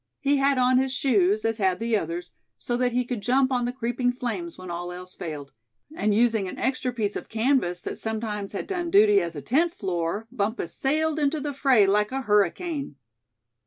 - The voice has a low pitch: No, high, 230 Hz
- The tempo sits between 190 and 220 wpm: Yes, average, 200 wpm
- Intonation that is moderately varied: Yes, average, 5.0 semitones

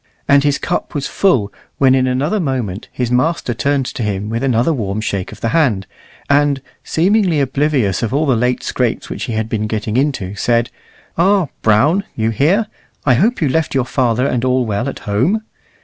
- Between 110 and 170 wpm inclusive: No, average, 195 wpm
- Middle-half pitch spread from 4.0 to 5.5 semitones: Yes, average, 4.7 semitones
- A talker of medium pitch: No, low, 130 Hz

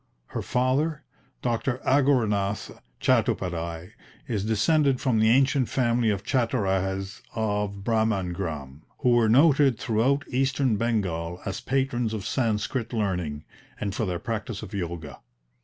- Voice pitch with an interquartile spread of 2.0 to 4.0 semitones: No, average, 4.8 semitones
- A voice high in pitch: No, low, 110 Hz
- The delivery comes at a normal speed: No, slow, 125 wpm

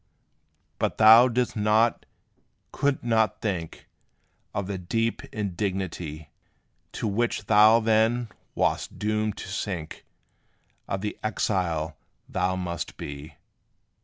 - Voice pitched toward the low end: Yes, low, 105 Hz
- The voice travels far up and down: No, average, 3.6 semitones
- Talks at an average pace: No, slow, 105 wpm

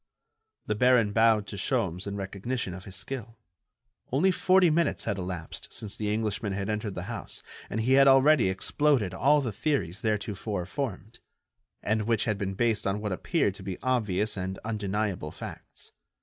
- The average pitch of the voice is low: Yes, low, 105 Hz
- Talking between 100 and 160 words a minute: No, average, 170 wpm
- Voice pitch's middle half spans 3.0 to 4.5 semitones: Yes, average, 4.1 semitones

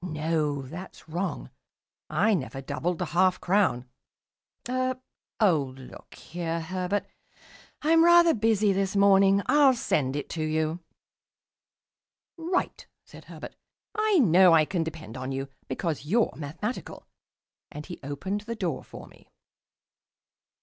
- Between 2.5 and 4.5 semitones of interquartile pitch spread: No, average, 5.3 semitones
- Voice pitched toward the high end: No, medium, 180 Hz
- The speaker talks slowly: Yes, slow, 130 wpm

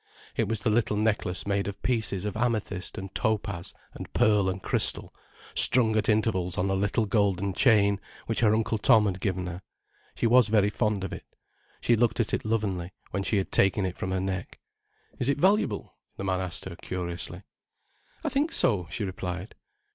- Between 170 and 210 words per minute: Yes, average, 190 wpm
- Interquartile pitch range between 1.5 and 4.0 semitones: Yes, average, 2.9 semitones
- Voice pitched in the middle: No, low, 100 Hz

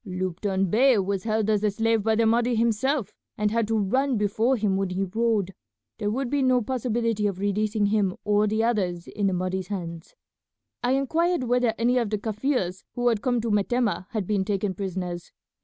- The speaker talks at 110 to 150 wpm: No, average, 195 wpm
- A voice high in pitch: Yes, high, 215 Hz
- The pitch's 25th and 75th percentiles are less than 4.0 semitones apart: Yes, average, 3.3 semitones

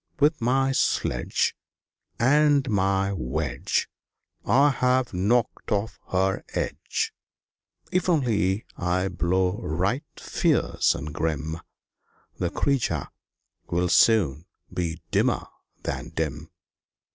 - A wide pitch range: Yes, wide, 6.6 semitones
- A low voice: Yes, low, 100 Hz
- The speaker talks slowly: Yes, slow, 100 wpm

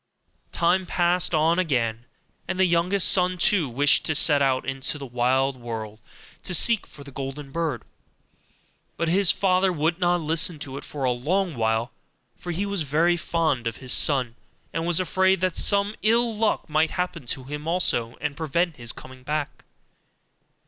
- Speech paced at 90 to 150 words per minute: No, average, 175 wpm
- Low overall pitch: No, medium, 160 Hz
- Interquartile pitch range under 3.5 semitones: No, average, 5.2 semitones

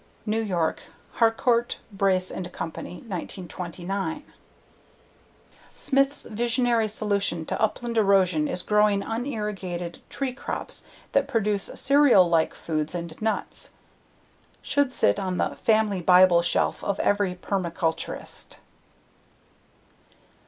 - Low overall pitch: No, high, 200 Hz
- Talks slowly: Yes, slow, 105 wpm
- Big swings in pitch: No, average, 4.1 semitones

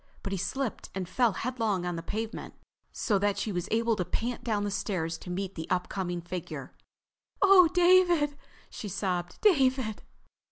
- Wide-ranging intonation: Yes, wide, 5.9 semitones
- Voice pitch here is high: Yes, high, 205 Hz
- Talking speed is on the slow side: No, average, 165 wpm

